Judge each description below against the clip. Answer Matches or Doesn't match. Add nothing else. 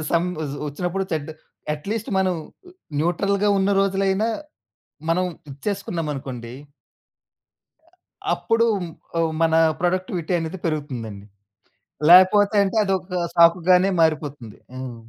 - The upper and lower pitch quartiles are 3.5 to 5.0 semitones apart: Matches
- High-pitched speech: Doesn't match